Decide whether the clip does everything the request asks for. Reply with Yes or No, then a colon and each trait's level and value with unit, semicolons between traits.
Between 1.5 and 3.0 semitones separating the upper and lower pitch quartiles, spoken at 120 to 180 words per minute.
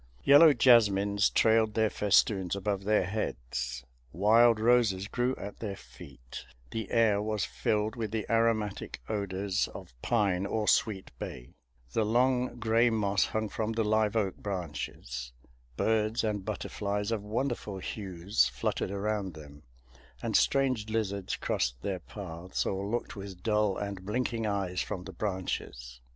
Yes: average, 2.7 semitones; average, 140 wpm